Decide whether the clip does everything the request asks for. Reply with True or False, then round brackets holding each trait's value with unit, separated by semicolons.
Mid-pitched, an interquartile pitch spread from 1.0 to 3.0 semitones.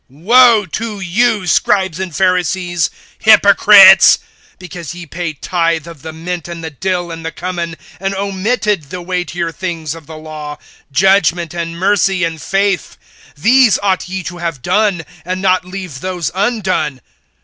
True (180 Hz; 2.7 semitones)